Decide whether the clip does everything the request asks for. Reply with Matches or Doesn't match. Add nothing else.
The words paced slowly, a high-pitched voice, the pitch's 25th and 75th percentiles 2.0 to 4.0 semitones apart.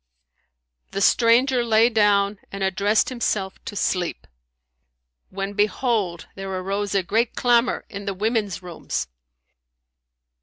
Matches